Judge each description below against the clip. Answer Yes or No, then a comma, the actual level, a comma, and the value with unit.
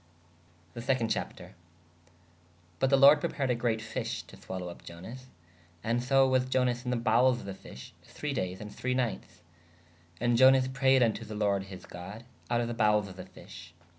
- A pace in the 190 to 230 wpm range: Yes, average, 195 wpm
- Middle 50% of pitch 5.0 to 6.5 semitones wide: No, average, 4.6 semitones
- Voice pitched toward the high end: No, low, 115 Hz